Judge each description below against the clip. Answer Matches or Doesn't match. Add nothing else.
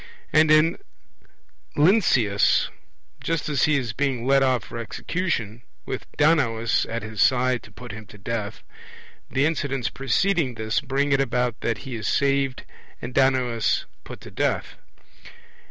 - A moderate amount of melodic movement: Matches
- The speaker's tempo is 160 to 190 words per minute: Doesn't match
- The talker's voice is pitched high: Doesn't match